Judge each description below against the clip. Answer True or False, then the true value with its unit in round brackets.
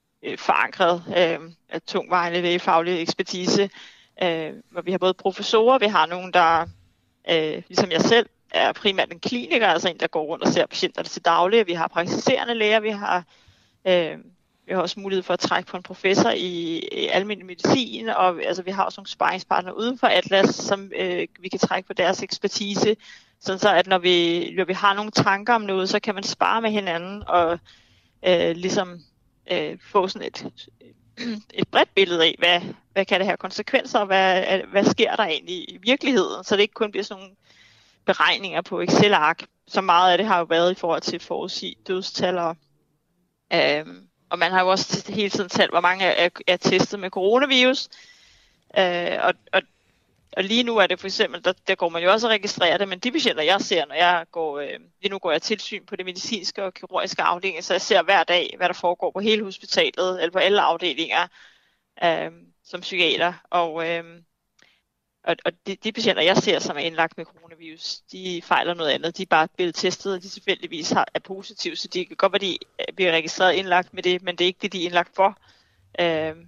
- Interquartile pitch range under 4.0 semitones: True (3.1 semitones)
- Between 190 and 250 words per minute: True (205 wpm)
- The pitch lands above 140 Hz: True (185 Hz)